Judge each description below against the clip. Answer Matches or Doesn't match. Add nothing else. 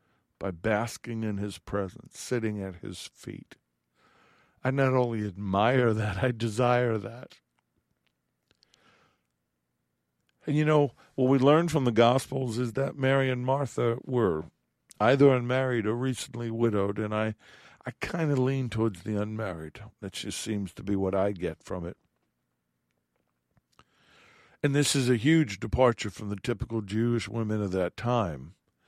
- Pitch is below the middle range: Matches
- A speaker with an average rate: Matches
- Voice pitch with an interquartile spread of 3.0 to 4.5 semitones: Doesn't match